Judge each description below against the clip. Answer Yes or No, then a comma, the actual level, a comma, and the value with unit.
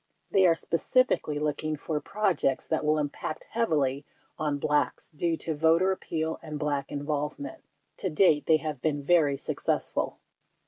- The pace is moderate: Yes, average, 165 wpm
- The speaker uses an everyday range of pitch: No, narrow, 2.3 semitones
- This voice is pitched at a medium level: Yes, medium, 155 Hz